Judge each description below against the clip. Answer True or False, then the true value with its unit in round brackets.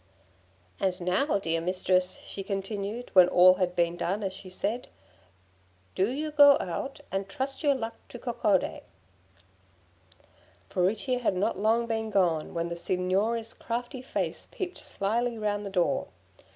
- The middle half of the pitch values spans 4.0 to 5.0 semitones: True (4.6 semitones)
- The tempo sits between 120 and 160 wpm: True (145 wpm)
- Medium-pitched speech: False (200 Hz)